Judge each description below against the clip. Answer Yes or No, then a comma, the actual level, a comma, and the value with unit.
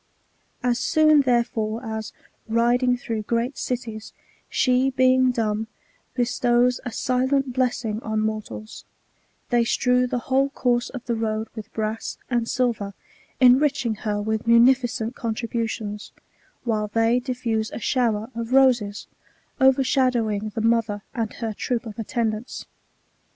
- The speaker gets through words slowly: Yes, slow, 130 wpm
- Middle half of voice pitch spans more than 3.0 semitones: No, narrow, 2.4 semitones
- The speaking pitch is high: Yes, high, 235 Hz